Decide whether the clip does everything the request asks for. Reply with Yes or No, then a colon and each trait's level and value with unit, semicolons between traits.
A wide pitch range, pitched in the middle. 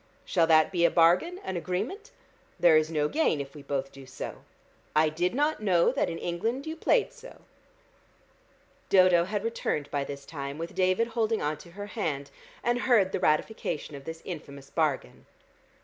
Yes: wide, 6.2 semitones; medium, 170 Hz